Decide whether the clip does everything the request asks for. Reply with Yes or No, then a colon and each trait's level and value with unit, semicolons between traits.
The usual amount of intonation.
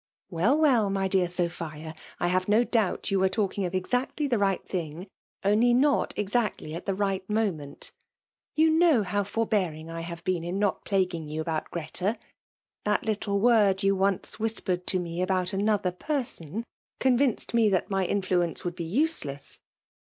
Yes: average, 3.9 semitones